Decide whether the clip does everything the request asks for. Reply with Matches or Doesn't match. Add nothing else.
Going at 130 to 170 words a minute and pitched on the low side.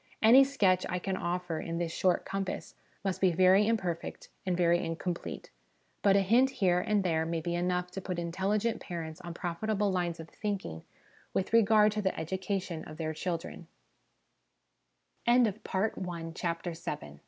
Doesn't match